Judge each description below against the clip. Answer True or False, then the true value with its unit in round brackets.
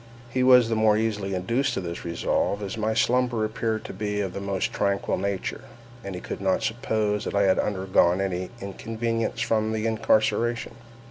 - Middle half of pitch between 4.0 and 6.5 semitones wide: False (2.6 semitones)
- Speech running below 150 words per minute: False (185 wpm)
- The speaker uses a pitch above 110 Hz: False (105 Hz)